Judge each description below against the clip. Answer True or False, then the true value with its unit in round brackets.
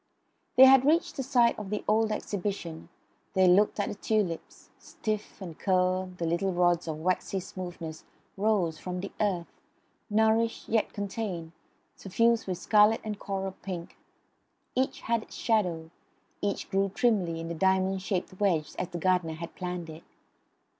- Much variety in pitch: False (3.4 semitones)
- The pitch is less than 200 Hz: True (190 Hz)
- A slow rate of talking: False (155 wpm)